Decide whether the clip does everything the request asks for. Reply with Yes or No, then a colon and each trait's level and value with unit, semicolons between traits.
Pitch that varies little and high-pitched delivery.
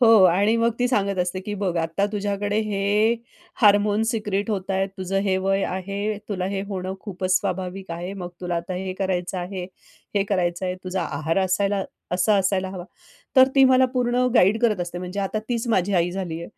Yes: narrow, 2.2 semitones; high, 195 Hz